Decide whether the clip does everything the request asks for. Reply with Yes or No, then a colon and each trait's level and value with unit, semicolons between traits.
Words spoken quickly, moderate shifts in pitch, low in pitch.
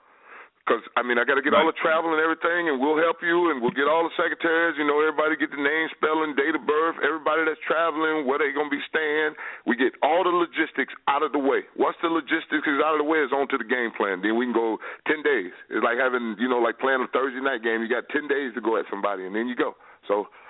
No: fast, 270 wpm; average, 3.9 semitones; medium, 155 Hz